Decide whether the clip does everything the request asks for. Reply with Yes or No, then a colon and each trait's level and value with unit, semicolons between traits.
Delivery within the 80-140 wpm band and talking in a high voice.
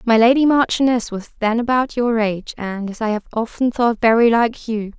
No: fast, 205 wpm; high, 230 Hz